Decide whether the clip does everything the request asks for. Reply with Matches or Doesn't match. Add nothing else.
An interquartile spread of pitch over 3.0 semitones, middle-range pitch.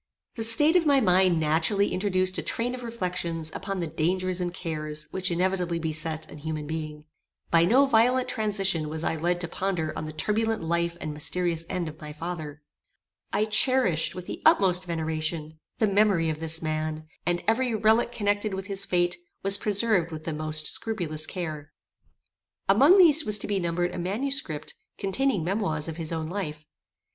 Matches